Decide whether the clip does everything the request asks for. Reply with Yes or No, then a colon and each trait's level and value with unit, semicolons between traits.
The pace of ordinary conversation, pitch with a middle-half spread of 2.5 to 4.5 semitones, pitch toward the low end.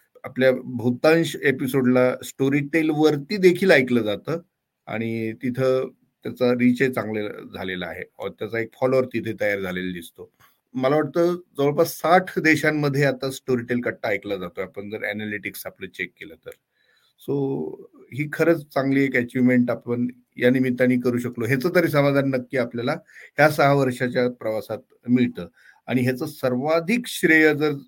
No: fast, 140 wpm; average, 3.6 semitones; low, 130 Hz